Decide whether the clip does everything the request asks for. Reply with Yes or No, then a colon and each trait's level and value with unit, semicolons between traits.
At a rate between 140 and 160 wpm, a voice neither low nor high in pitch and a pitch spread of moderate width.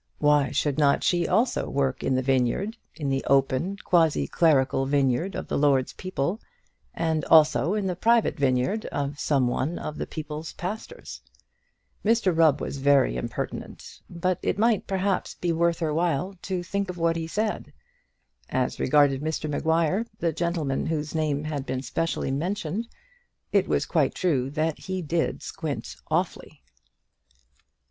Yes: average, 155 wpm; medium, 160 Hz; average, 4.5 semitones